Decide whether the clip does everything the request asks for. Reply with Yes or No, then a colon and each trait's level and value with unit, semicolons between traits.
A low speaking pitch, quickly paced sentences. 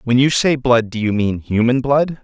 Yes: low, 125 Hz; fast, 240 wpm